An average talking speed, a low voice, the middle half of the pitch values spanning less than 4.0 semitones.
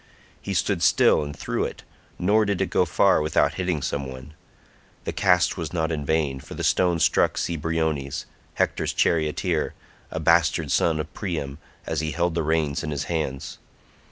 Yes: average, 175 wpm; very low, 80 Hz; narrow, 2.6 semitones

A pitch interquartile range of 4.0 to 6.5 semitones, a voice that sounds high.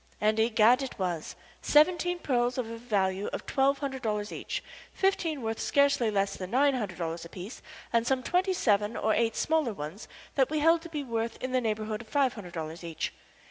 Yes: average, 5.3 semitones; high, 230 Hz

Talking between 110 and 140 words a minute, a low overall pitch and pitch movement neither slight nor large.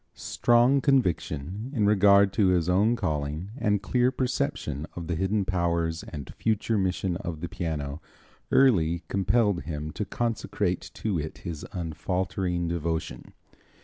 Yes: slow, 135 wpm; very low, 90 Hz; average, 4.3 semitones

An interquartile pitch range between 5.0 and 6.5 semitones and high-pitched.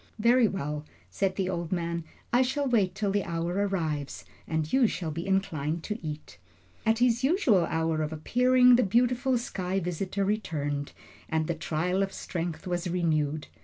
No: average, 5.3 semitones; medium, 180 Hz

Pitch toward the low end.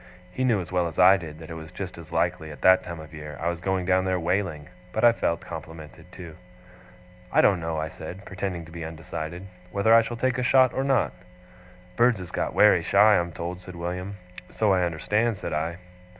Yes: very low, 90 Hz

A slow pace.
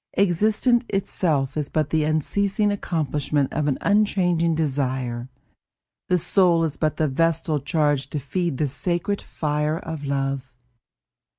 Yes: slow, 130 wpm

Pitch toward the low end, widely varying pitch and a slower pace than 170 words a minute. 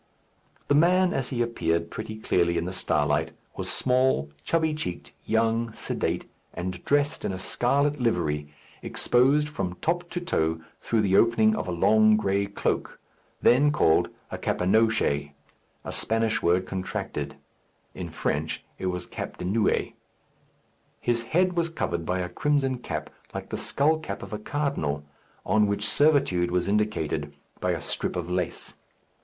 Yes: low, 110 Hz; wide, 7.7 semitones; average, 155 wpm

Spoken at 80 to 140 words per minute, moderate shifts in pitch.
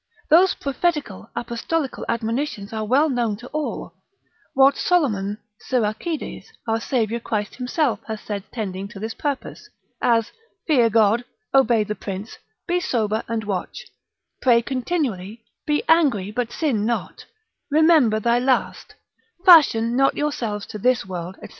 Yes: slow, 135 wpm; average, 4.7 semitones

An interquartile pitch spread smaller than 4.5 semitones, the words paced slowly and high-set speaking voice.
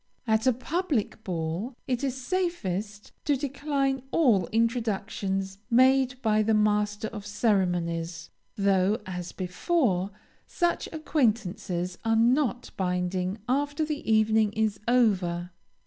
No: average, 5.2 semitones; slow, 115 wpm; high, 220 Hz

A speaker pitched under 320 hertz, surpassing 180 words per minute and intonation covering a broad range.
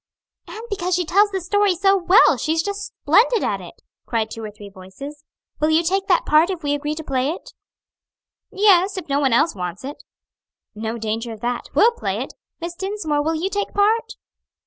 No: very high, 330 Hz; average, 200 wpm; wide, 6.7 semitones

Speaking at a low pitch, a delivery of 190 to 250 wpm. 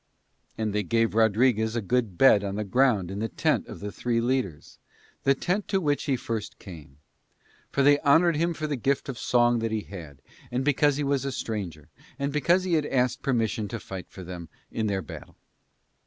Yes: low, 115 Hz; fast, 205 wpm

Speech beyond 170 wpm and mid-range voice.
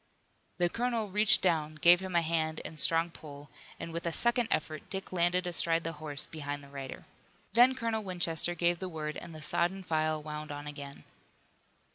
Yes: average, 190 wpm; medium, 165 Hz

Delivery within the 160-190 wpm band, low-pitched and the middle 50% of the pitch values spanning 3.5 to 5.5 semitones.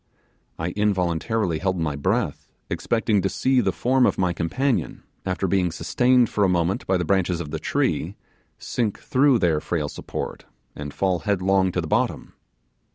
Yes: average, 165 wpm; very low, 95 Hz; average, 4.2 semitones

